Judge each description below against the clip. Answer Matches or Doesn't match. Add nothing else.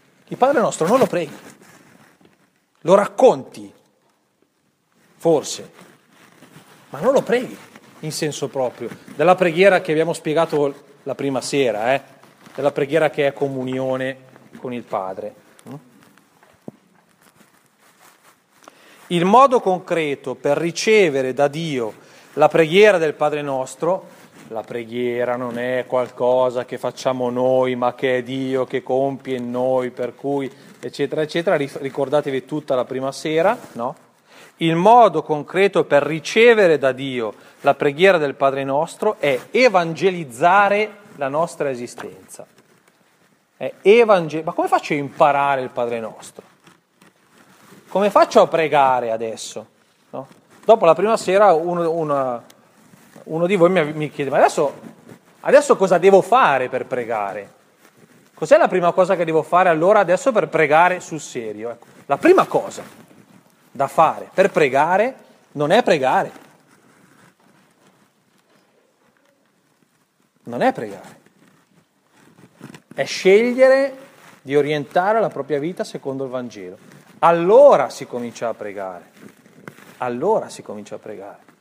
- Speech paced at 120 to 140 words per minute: Matches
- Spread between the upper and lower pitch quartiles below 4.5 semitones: Doesn't match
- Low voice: Doesn't match